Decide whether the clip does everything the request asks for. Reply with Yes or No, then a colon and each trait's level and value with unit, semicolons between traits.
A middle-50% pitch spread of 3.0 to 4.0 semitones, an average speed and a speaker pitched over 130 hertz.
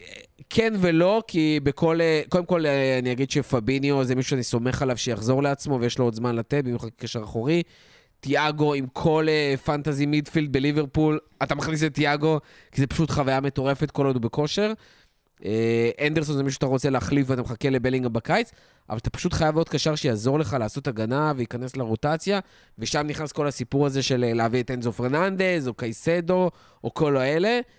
No: average, 3.4 semitones; fast, 175 wpm; medium, 140 Hz